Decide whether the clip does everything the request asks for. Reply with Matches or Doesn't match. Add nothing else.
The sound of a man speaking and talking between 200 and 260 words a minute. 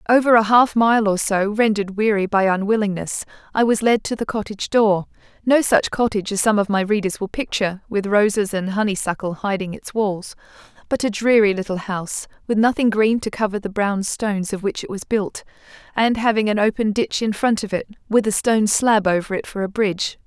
Doesn't match